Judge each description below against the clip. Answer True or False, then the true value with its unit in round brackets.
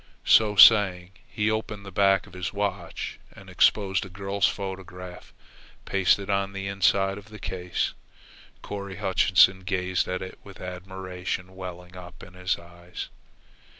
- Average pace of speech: True (145 wpm)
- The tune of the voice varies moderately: False (1.5 semitones)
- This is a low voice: True (95 Hz)